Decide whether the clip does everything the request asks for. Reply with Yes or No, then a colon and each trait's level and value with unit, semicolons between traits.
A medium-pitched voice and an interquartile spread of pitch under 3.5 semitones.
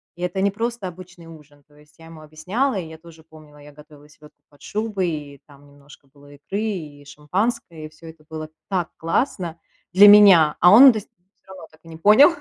No: medium, 160 Hz; average, 4.3 semitones